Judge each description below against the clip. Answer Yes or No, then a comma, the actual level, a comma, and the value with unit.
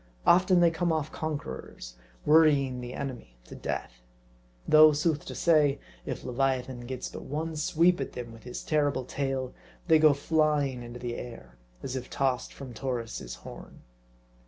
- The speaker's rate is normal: Yes, average, 160 wpm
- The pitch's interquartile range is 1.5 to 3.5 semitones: No, average, 3.9 semitones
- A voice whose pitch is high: No, low, 135 Hz